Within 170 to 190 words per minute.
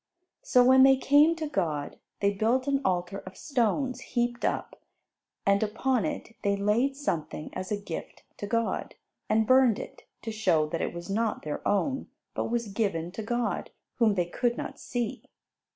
Yes: average, 175 wpm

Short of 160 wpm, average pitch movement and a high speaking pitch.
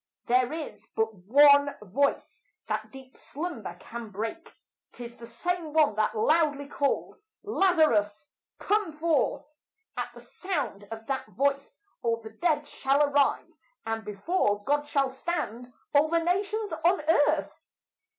No: slow, 135 wpm; wide, 6.0 semitones; very high, 280 Hz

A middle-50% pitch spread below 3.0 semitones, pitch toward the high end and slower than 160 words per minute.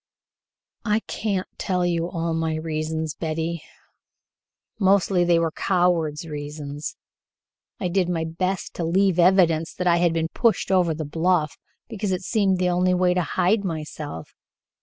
No: narrow, 2.4 semitones; medium, 170 Hz; average, 150 wpm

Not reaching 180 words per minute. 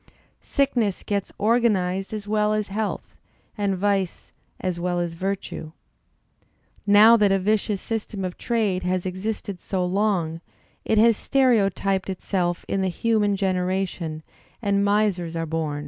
Yes: slow, 135 wpm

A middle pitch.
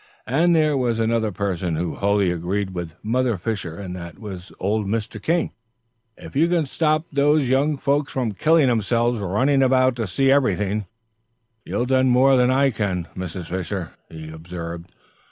No: low, 110 Hz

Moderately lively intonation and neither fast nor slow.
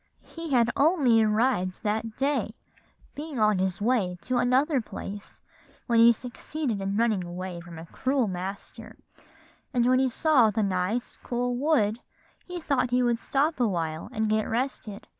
Yes: average, 4.2 semitones; average, 160 wpm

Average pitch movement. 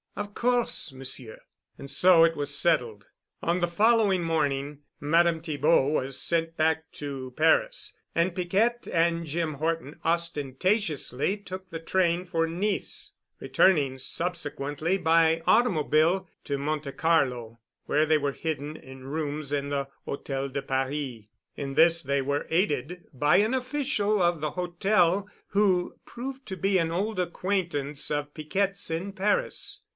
Yes: average, 4.4 semitones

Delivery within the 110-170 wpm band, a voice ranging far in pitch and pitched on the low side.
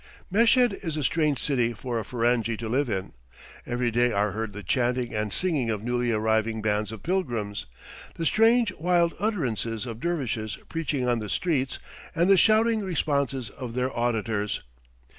Yes: average, 165 wpm; wide, 6.8 semitones; low, 120 Hz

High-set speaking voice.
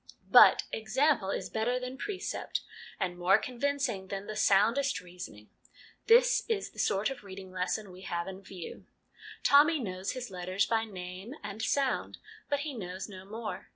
Yes: high, 210 Hz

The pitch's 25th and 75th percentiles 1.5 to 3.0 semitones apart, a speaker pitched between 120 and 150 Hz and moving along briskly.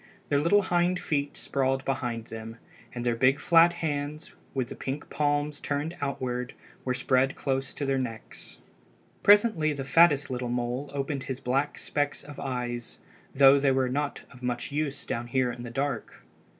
No: average, 2.7 semitones; low, 135 Hz; average, 170 wpm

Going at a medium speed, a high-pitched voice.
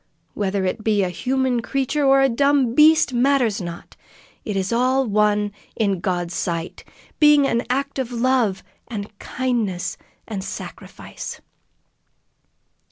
No: slow, 130 wpm; high, 235 Hz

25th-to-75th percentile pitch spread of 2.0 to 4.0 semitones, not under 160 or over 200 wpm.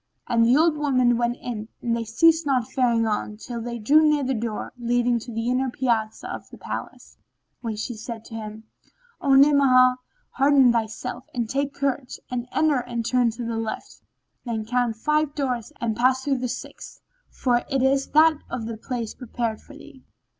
Yes: average, 2.9 semitones; average, 190 wpm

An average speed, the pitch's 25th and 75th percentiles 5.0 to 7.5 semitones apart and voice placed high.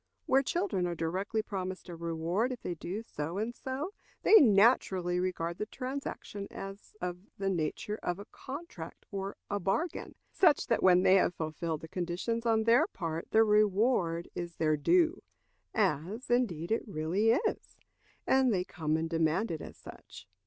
Yes: average, 165 wpm; average, 5.3 semitones; high, 195 Hz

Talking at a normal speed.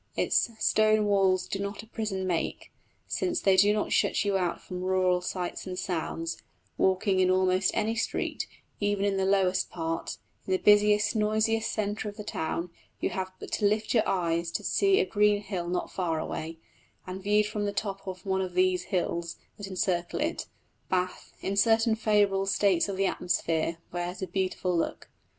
Yes: average, 185 wpm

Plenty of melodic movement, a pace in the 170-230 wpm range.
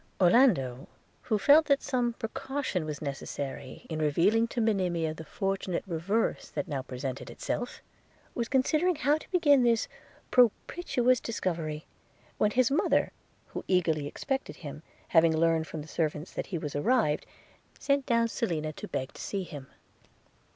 No: wide, 8.0 semitones; average, 150 wpm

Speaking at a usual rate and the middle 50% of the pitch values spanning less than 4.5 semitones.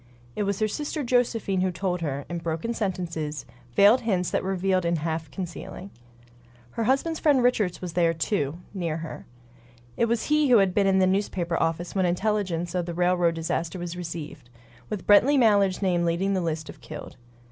Yes: average, 185 wpm; average, 3.5 semitones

